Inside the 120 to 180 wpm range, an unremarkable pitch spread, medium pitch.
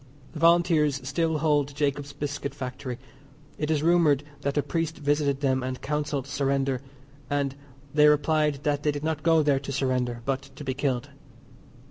No: average, 165 wpm; narrow, 1.8 semitones; medium, 145 Hz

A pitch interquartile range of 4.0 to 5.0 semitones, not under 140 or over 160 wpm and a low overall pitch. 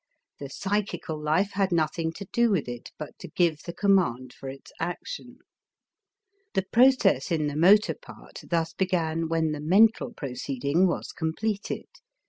No: average, 4.5 semitones; average, 150 wpm; medium, 165 Hz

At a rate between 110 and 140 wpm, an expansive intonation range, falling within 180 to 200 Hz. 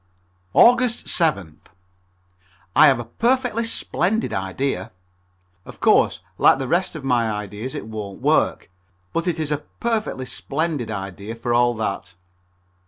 No: slow, 135 wpm; wide, 8.2 semitones; low, 130 Hz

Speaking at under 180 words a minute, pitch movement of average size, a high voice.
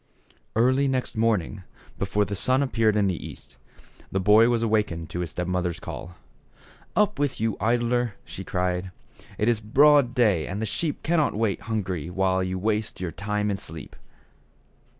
No: average, 170 wpm; average, 4.4 semitones; low, 105 Hz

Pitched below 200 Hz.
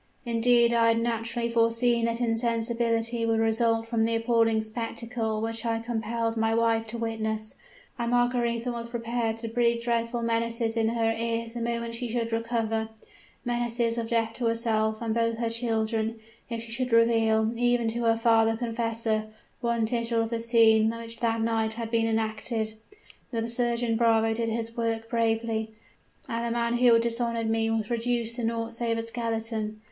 No: high, 230 Hz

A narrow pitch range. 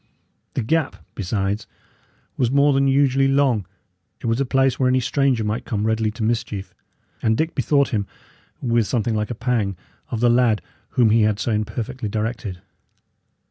No: average, 3.6 semitones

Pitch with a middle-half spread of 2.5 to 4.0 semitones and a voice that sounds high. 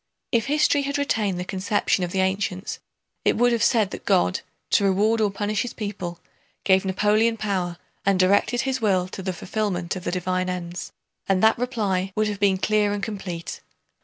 Yes: average, 2.8 semitones; high, 200 Hz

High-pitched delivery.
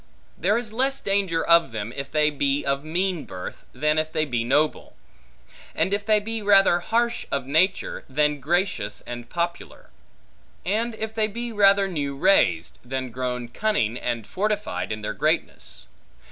No: medium, 160 Hz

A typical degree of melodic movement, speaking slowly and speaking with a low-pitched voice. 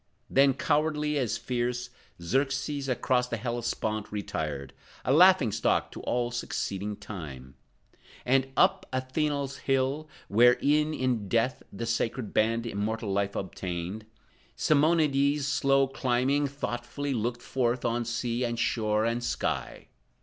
Yes: average, 3.7 semitones; slow, 125 wpm; low, 125 Hz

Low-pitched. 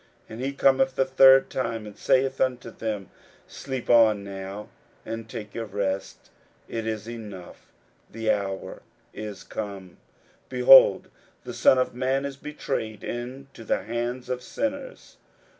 Yes: low, 115 Hz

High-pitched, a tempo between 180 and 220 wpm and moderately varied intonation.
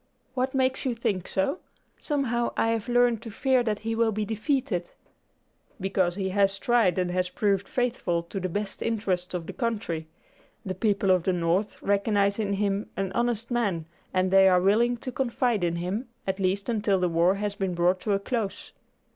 Yes: high, 200 Hz; average, 195 wpm; average, 3.8 semitones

